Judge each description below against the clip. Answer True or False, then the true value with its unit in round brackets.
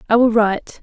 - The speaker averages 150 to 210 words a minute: False (220 wpm)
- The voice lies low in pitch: False (220 Hz)